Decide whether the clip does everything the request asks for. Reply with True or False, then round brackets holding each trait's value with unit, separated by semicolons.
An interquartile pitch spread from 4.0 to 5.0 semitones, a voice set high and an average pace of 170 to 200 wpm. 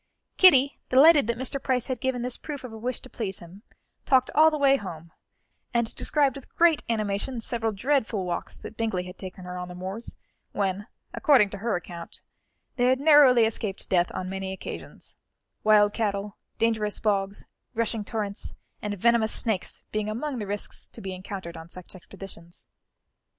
True (4.7 semitones; 215 Hz; 175 wpm)